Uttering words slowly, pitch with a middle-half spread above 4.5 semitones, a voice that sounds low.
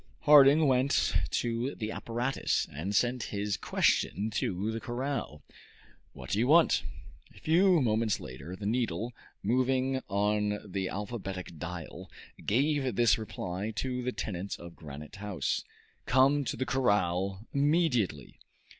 Yes: slow, 130 wpm; average, 5.2 semitones; low, 110 Hz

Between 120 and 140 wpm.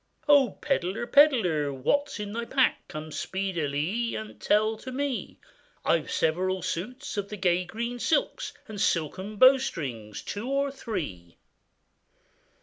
Yes: slow, 135 wpm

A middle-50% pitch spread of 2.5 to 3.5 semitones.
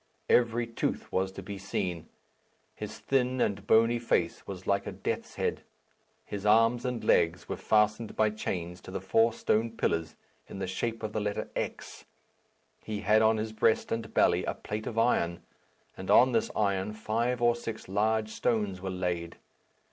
Yes: average, 2.9 semitones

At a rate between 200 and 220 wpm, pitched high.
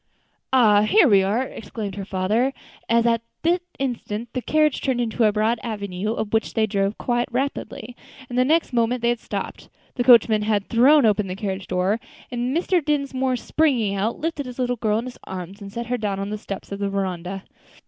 Yes: fast, 205 wpm; high, 230 Hz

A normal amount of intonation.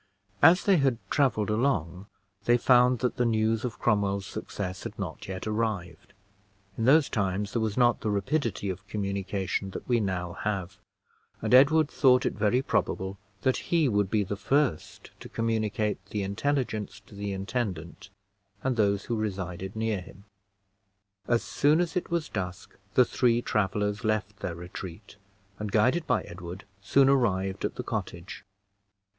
Yes: average, 4.1 semitones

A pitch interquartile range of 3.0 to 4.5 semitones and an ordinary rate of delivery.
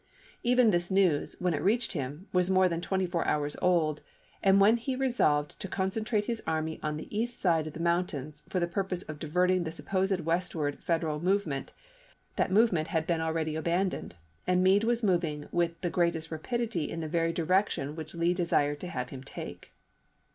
Yes: average, 3.4 semitones; average, 190 wpm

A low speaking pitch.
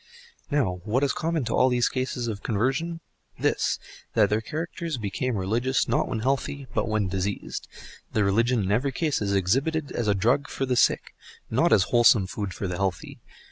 Yes: low, 120 Hz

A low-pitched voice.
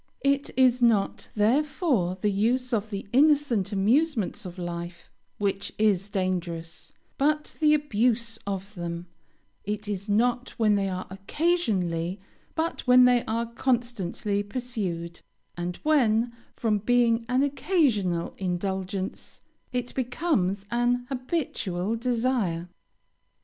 No: high, 220 Hz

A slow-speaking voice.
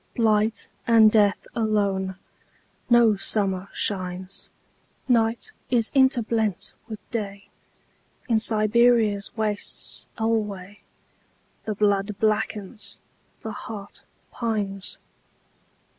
Yes: slow, 70 wpm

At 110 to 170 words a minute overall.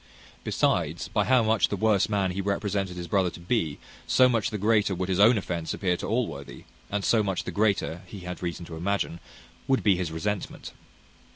No: average, 200 wpm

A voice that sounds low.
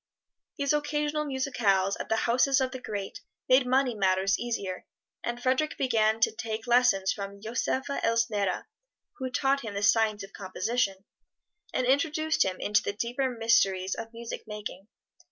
No: high, 230 Hz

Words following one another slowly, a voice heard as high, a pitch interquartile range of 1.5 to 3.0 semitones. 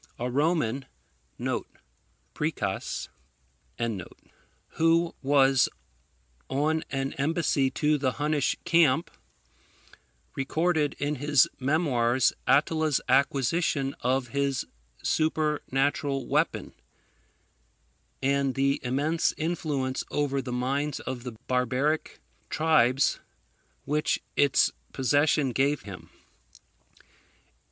No: slow, 80 wpm; medium, 140 Hz; narrow, 2.6 semitones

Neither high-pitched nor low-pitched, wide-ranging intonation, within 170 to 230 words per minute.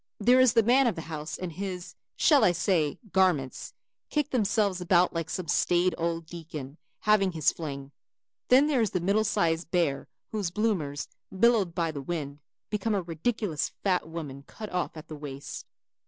No: medium, 175 Hz; average, 4.9 semitones; average, 175 wpm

